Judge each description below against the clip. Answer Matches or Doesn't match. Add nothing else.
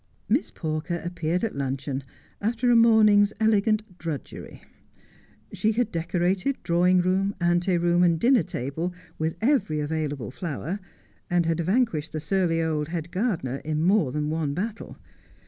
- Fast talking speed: Doesn't match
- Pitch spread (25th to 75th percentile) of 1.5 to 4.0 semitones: Doesn't match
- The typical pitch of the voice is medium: Matches